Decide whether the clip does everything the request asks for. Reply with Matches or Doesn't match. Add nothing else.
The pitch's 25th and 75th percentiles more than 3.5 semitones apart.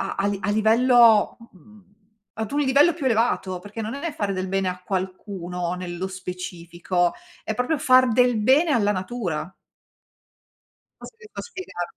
Matches